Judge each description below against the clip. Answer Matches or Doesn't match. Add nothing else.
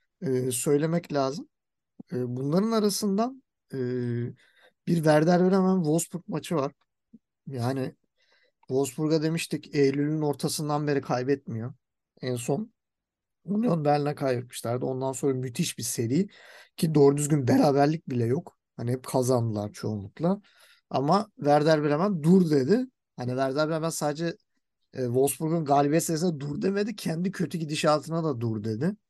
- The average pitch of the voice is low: Doesn't match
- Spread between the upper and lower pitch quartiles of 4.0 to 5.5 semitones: Matches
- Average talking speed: Matches